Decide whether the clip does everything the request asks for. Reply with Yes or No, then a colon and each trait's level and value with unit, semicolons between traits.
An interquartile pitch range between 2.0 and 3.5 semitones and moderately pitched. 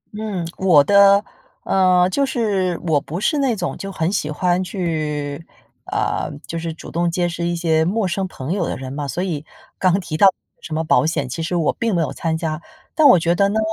Yes: average, 3.2 semitones; medium, 175 Hz